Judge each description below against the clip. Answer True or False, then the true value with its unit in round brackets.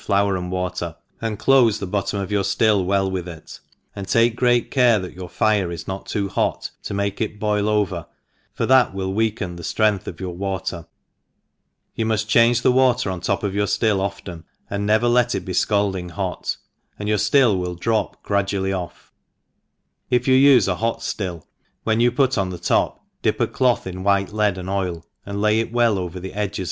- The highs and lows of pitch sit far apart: False (3.1 semitones)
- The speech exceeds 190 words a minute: True (205 wpm)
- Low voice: True (100 Hz)